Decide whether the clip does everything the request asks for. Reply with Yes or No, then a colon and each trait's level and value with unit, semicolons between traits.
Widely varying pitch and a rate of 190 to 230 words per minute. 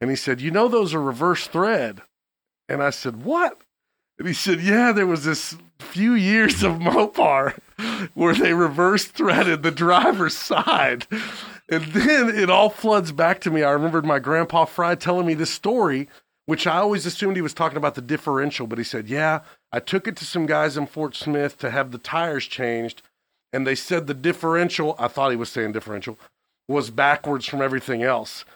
No: average, 4.7 semitones; average, 195 wpm